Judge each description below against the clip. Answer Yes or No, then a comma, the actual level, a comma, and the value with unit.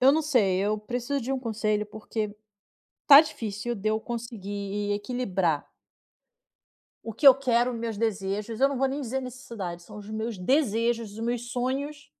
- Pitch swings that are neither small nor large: Yes, average, 3.6 semitones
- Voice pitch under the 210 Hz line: No, high, 230 Hz